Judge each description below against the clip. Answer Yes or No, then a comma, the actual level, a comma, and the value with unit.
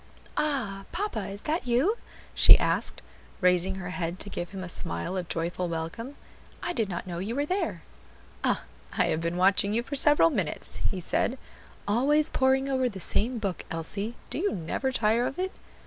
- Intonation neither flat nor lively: No, wide, 6.7 semitones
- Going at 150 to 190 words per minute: Yes, average, 185 wpm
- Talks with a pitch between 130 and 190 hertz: No, high, 205 Hz